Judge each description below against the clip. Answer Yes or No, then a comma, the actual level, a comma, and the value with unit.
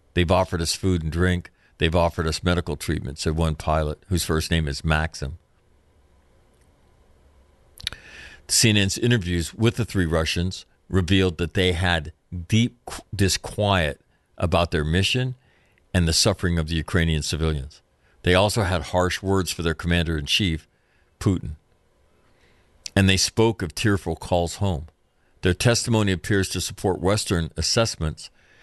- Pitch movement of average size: Yes, average, 3.3 semitones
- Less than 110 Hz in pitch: Yes, very low, 90 Hz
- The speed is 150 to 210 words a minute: No, average, 140 wpm